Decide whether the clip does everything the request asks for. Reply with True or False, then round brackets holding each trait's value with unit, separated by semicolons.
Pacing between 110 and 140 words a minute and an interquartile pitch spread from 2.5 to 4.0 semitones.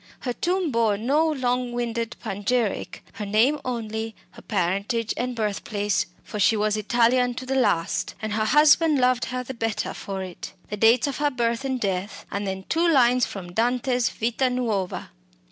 False (175 wpm; 3.3 semitones)